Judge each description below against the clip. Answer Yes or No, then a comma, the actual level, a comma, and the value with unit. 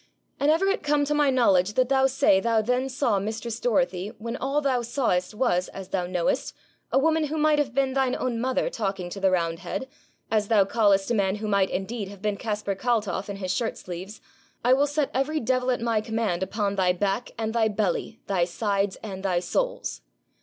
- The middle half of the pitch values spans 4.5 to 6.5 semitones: Yes, average, 5.0 semitones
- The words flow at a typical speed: No, fast, 210 wpm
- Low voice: No, high, 220 Hz